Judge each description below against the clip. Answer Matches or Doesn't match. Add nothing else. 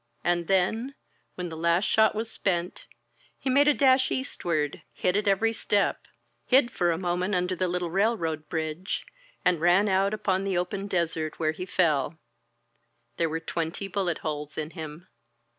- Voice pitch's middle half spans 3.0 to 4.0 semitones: Matches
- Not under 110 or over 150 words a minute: Doesn't match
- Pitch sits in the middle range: Matches